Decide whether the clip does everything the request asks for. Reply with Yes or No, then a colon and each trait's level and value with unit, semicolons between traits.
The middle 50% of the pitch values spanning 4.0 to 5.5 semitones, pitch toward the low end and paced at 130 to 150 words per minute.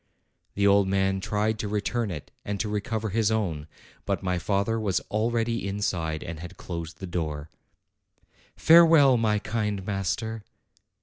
No: average, 3.3 semitones; low, 100 Hz; average, 145 wpm